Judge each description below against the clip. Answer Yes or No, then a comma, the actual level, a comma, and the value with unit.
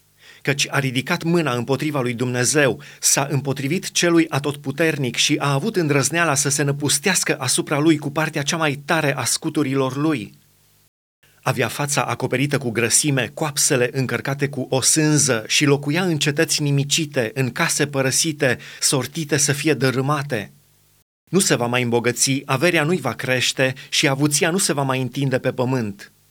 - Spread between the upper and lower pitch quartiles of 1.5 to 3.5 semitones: Yes, average, 2.9 semitones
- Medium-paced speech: Yes, average, 155 wpm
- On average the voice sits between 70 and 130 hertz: No, medium, 140 Hz